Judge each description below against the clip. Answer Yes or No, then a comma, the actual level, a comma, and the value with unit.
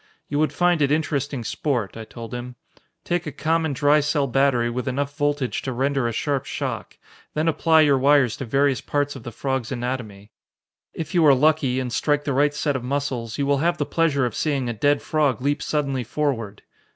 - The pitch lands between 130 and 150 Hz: Yes, medium, 140 Hz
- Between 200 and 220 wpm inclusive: Yes, fast, 205 wpm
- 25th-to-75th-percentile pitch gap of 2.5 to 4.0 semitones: Yes, average, 2.9 semitones